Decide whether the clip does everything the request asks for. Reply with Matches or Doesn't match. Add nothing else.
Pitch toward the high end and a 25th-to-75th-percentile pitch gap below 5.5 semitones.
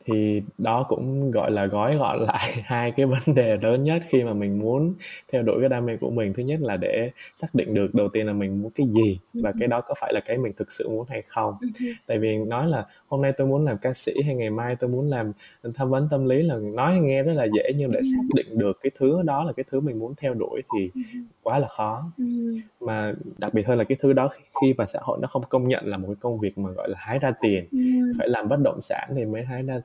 Doesn't match